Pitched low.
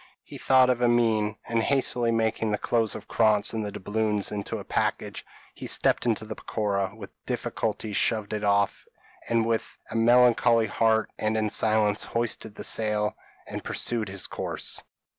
Yes: low, 110 Hz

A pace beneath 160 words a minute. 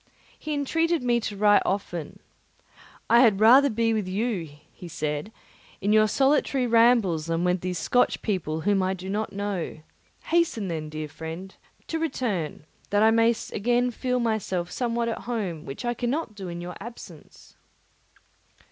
No: average, 165 wpm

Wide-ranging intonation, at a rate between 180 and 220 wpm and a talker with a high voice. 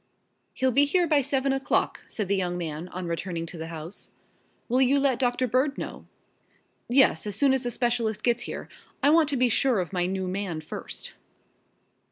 Yes: wide, 6.7 semitones; average, 195 wpm; high, 240 Hz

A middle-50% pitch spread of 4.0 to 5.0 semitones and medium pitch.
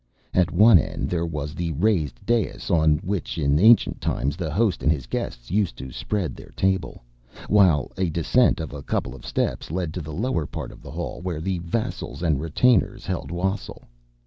No: average, 4.4 semitones; very low, 85 Hz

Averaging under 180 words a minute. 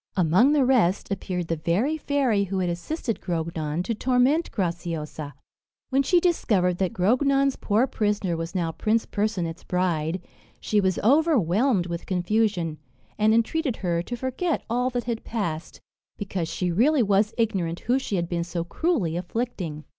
Yes: average, 155 wpm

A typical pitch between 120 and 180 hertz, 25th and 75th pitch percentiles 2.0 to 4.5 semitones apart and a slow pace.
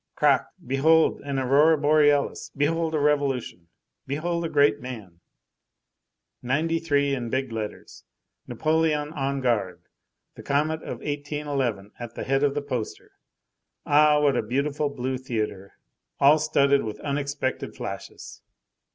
Yes: medium, 140 Hz; average, 3.0 semitones; slow, 130 wpm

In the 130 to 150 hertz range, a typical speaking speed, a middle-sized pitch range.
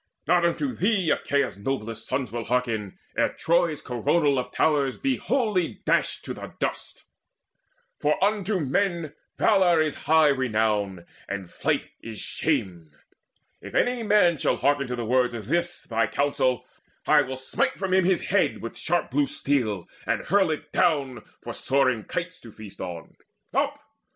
No: medium, 140 Hz; average, 160 wpm; wide, 6.7 semitones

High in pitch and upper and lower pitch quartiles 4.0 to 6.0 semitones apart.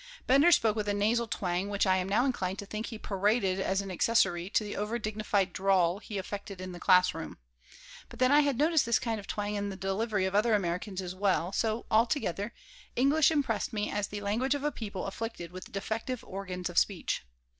No: high, 205 Hz; average, 3.1 semitones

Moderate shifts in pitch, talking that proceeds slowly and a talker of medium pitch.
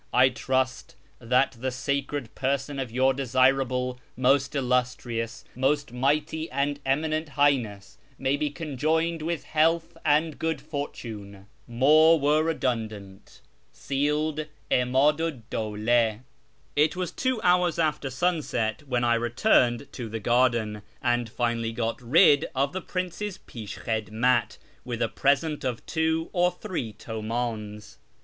No: average, 4.4 semitones; slow, 125 wpm; low, 130 Hz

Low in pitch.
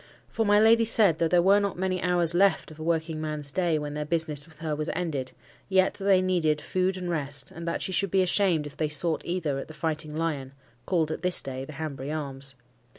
No: medium, 165 Hz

